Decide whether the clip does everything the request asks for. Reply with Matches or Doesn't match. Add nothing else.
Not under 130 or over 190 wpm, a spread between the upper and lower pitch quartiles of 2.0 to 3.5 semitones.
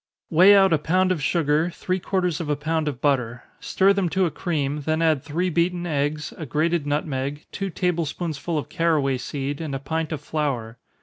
Doesn't match